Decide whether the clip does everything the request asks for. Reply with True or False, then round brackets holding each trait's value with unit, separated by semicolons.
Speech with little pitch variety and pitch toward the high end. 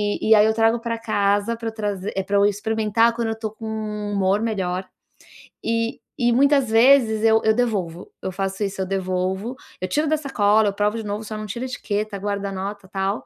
True (2.2 semitones; 210 Hz)